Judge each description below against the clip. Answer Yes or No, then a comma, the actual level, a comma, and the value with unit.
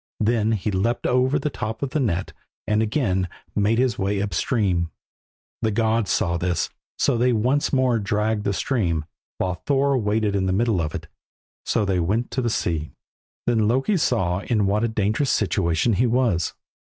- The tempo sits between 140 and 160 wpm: No, average, 185 wpm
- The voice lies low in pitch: Yes, low, 110 Hz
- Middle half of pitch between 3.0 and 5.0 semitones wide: Yes, average, 4.0 semitones